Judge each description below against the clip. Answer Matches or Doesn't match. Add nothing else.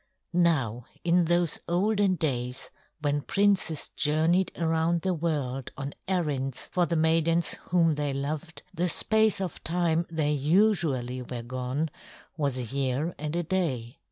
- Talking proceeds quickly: Doesn't match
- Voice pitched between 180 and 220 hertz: Doesn't match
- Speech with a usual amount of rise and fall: Matches